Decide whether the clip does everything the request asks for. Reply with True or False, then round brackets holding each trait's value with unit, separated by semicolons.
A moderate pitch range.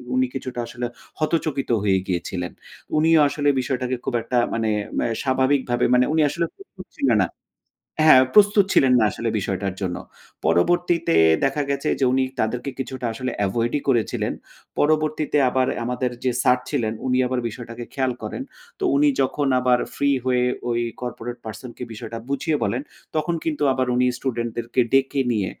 True (3.3 semitones)